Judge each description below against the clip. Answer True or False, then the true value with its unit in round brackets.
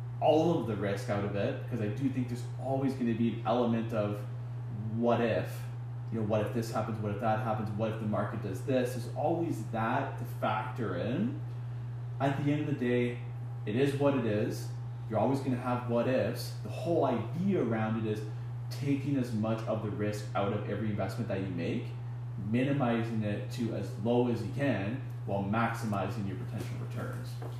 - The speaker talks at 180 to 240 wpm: True (200 wpm)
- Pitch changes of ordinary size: False (1.7 semitones)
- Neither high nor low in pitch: False (120 Hz)